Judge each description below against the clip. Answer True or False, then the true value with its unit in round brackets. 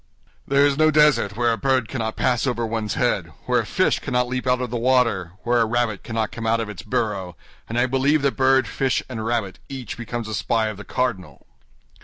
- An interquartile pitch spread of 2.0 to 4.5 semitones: True (2.9 semitones)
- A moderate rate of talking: False (225 wpm)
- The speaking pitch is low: True (120 Hz)